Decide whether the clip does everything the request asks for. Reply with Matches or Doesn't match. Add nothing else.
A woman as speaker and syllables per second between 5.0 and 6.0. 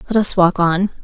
Matches